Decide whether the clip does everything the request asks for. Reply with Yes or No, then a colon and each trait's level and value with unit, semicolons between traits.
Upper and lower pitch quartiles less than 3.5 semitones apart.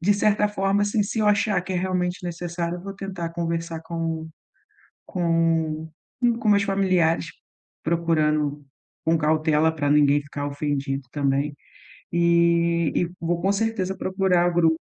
Yes: average, 3.0 semitones